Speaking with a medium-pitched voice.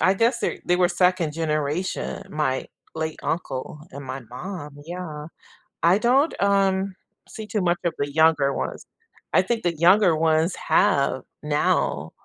Yes: medium, 170 Hz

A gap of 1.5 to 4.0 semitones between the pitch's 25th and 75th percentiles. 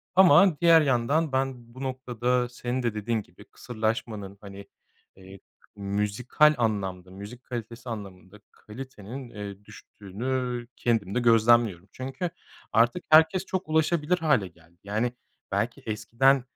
No: average, 4.4 semitones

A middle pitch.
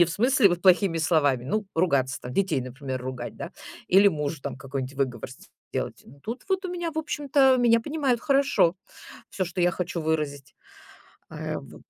Yes: medium, 175 Hz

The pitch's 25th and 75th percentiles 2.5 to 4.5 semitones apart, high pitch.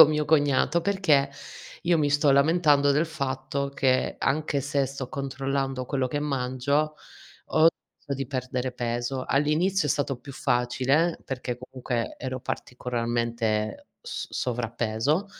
No: average, 2.8 semitones; low, 135 Hz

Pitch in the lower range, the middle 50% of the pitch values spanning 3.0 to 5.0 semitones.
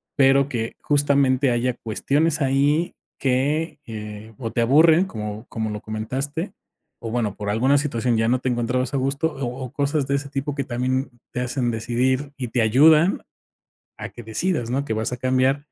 Yes: low, 130 Hz; average, 3.4 semitones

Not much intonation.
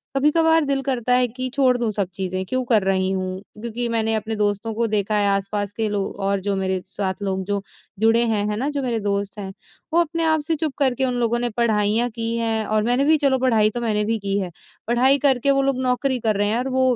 No: average, 4.1 semitones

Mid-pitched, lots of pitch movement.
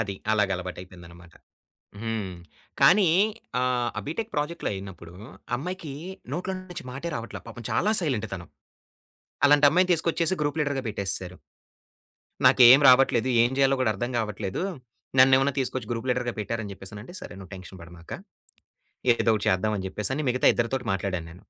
No: low, 120 Hz; wide, 6.6 semitones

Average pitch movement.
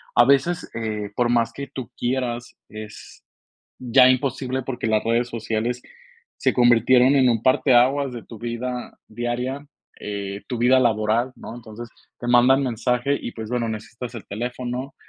No: narrow, 2.0 semitones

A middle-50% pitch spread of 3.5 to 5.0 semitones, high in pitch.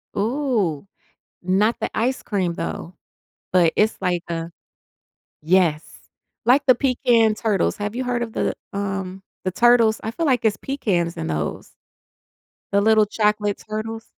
Yes: average, 4.2 semitones; high, 210 Hz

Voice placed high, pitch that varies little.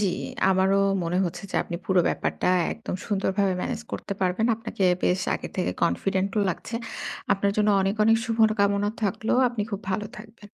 Yes: high, 200 Hz; narrow, 2.1 semitones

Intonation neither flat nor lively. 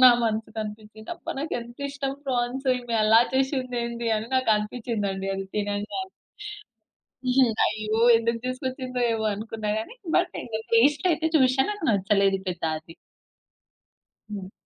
Yes: average, 3.6 semitones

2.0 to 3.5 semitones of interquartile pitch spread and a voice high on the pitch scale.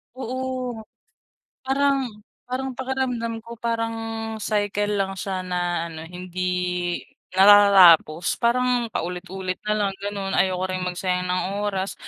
No: average, 4.2 semitones; high, 205 Hz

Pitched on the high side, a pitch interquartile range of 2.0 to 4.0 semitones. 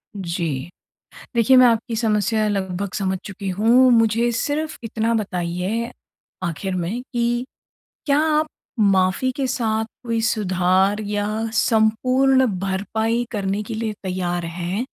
Yes: high, 215 Hz; average, 3.7 semitones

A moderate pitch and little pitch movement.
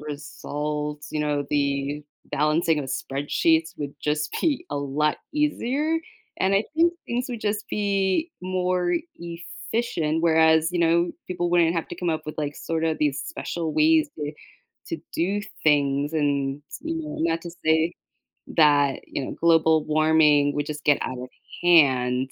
No: medium, 160 Hz; average, 3.4 semitones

